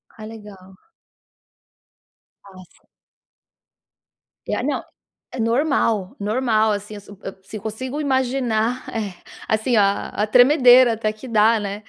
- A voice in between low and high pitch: No, high, 220 Hz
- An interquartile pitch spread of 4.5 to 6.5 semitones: No, average, 3.0 semitones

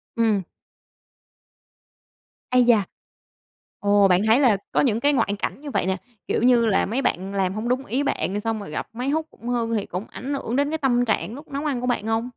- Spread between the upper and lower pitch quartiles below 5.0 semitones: Yes, average, 4.1 semitones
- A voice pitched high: Yes, high, 235 Hz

